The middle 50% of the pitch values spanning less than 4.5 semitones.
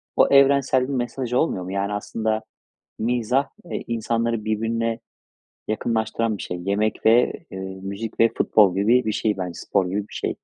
Yes: narrow, 2.4 semitones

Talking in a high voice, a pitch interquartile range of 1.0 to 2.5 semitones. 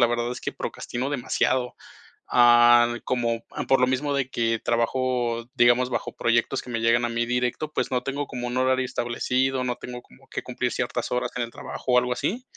No: low, 125 Hz; narrow, 1.4 semitones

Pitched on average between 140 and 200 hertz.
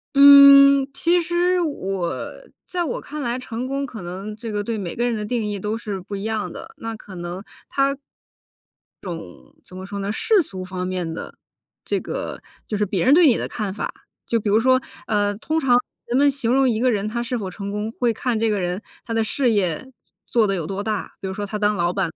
No: high, 220 Hz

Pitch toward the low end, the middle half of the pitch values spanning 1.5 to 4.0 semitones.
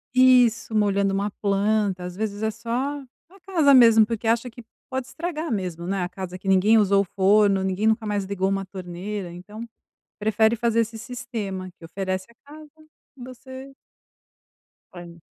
No: high, 210 Hz; average, 3.6 semitones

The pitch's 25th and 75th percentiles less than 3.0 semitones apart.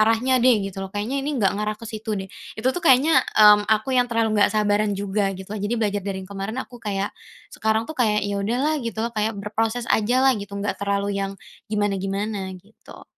Yes: narrow, 2.6 semitones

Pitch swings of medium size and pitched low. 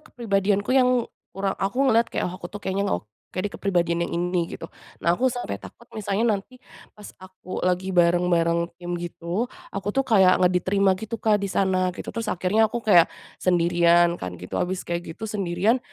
No: average, 3.3 semitones; high, 190 Hz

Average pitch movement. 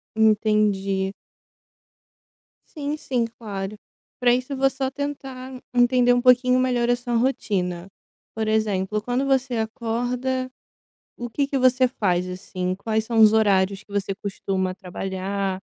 Yes: average, 4.5 semitones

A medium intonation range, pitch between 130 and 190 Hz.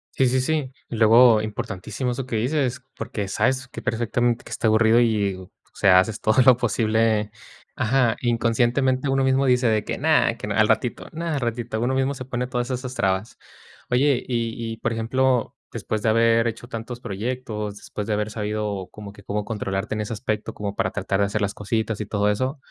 No: average, 3.0 semitones; low, 115 Hz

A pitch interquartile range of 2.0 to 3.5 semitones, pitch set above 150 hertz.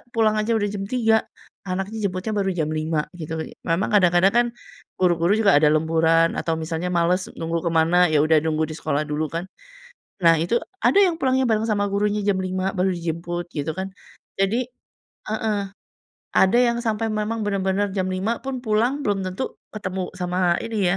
No: average, 4.3 semitones; high, 190 Hz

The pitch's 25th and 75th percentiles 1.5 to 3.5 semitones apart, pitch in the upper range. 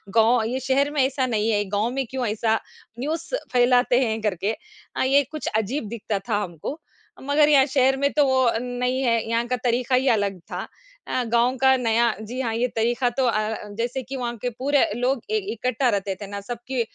Yes: average, 2.8 semitones; high, 245 Hz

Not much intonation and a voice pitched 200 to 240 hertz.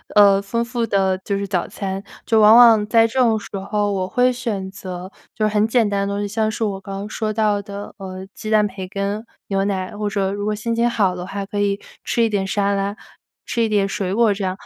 Yes: narrow, 1.9 semitones; high, 205 Hz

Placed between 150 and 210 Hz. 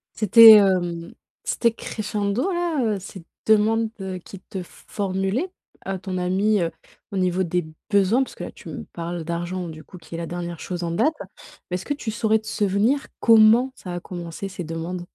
Yes: high, 190 Hz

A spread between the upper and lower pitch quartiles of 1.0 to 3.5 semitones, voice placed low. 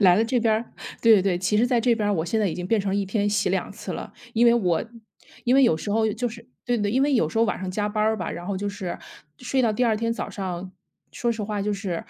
No: average, 3.2 semitones; high, 210 Hz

